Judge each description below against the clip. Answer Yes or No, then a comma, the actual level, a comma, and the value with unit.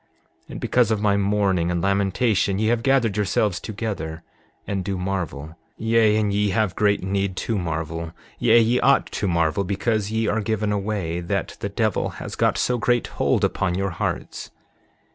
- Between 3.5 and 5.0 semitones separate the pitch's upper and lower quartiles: No, average, 3.0 semitones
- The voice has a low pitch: Yes, low, 100 Hz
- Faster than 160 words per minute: Yes, average, 180 wpm